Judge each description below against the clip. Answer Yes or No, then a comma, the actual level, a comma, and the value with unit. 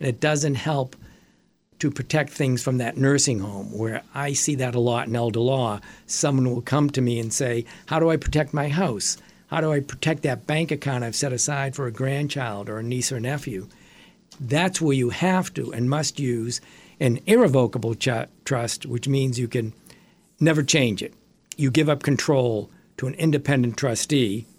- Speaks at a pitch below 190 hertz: Yes, low, 135 Hz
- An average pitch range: Yes, average, 3.7 semitones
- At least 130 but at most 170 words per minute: No, average, 190 wpm